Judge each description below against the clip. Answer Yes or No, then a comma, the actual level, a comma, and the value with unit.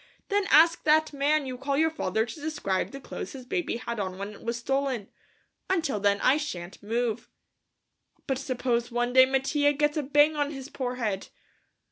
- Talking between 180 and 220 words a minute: Yes, average, 185 wpm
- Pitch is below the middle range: No, very high, 265 Hz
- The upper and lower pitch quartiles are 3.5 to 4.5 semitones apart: Yes, average, 3.9 semitones